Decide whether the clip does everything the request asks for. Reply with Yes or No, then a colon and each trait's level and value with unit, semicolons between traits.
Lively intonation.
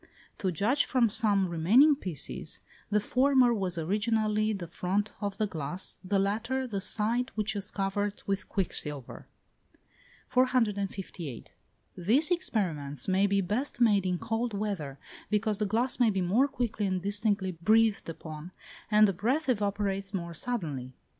No: average, 3.4 semitones